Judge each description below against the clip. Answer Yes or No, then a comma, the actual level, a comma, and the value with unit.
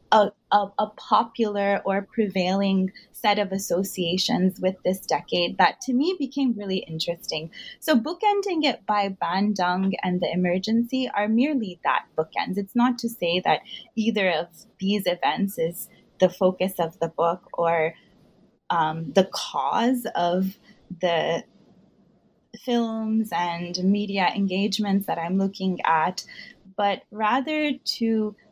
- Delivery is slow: Yes, slow, 130 wpm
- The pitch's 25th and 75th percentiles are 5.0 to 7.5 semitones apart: No, average, 3.5 semitones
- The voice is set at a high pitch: Yes, high, 200 Hz